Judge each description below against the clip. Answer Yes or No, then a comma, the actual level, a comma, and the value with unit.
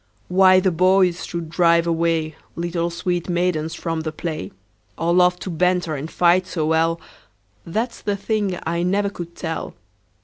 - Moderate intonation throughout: No, narrow, 1.8 semitones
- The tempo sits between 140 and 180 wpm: Yes, average, 165 wpm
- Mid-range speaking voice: Yes, medium, 170 Hz